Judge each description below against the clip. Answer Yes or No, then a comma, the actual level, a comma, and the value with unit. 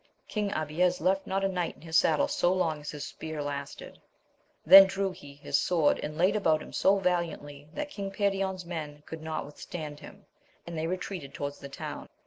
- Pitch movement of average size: Yes, average, 4.3 semitones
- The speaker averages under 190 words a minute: No, average, 195 wpm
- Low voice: No, medium, 170 Hz